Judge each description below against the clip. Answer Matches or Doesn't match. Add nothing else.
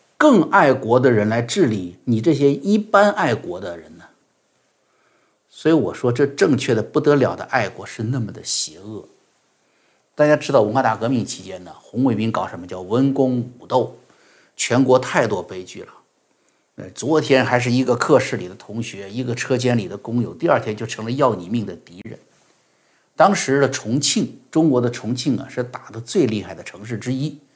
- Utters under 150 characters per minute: Doesn't match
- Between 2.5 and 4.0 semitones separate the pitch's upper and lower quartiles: Matches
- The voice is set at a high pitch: Doesn't match